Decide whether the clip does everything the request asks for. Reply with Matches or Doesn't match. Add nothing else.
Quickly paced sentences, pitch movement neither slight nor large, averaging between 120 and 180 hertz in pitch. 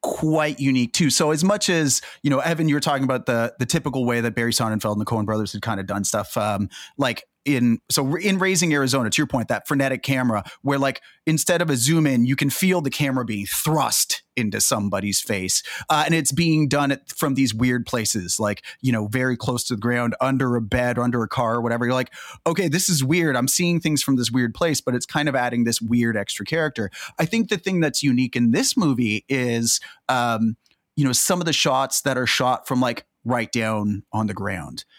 Matches